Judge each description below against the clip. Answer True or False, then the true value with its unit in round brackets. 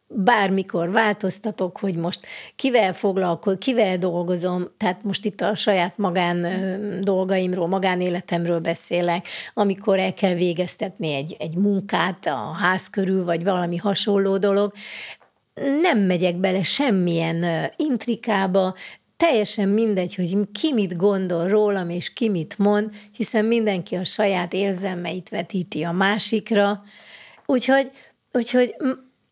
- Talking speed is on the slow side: False (115 wpm)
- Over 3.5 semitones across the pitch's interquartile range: False (2.7 semitones)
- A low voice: False (195 Hz)